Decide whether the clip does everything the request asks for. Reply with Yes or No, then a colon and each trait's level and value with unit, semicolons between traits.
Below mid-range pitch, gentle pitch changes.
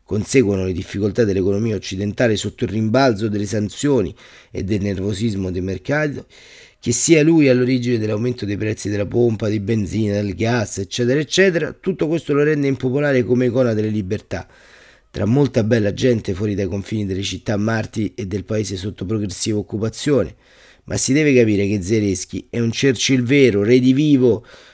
No: low, 110 Hz; average, 3.8 semitones